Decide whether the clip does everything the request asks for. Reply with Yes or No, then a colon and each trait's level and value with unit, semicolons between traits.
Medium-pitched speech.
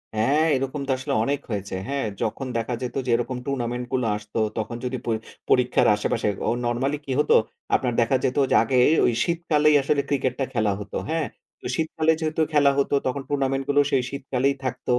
No: low, 130 Hz